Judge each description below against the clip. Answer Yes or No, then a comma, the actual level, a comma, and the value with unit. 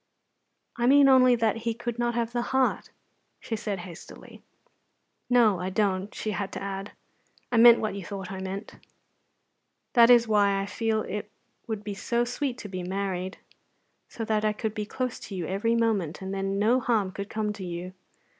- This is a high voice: Yes, high, 210 Hz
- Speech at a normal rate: Yes, average, 190 wpm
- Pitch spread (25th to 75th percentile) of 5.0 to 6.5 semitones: No, average, 3.3 semitones